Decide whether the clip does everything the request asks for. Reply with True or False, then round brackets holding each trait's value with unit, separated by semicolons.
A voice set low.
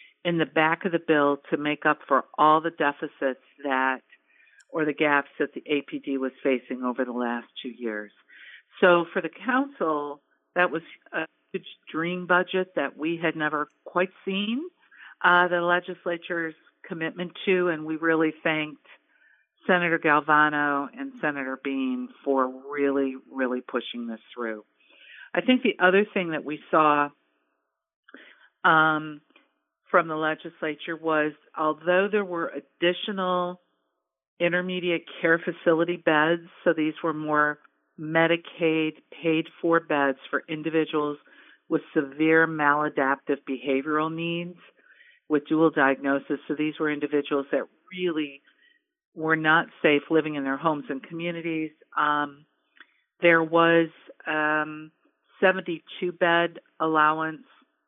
False (155 Hz)